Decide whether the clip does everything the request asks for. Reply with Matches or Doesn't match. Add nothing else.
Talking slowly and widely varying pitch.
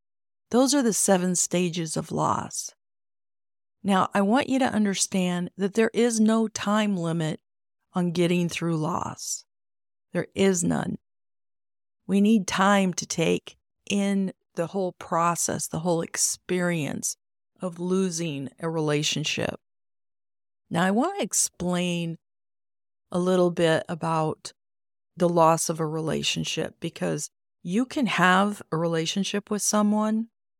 Doesn't match